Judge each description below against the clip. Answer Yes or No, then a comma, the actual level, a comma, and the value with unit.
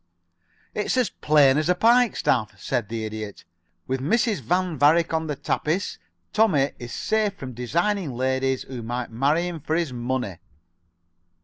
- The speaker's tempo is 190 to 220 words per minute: No, average, 155 wpm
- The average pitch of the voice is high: No, medium, 145 Hz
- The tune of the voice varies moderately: No, wide, 6.2 semitones